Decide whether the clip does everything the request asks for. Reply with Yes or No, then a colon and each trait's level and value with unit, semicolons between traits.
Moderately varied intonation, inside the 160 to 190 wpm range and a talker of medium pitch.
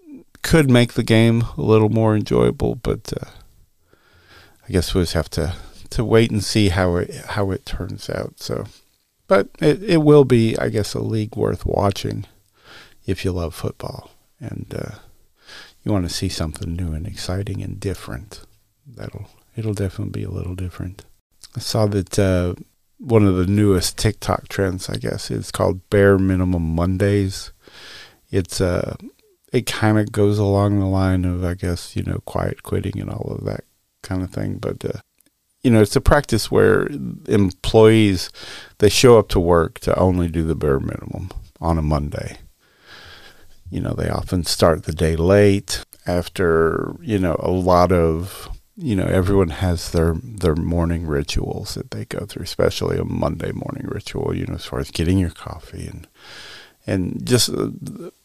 No: average, 3.5 semitones; average, 175 wpm; low, 100 Hz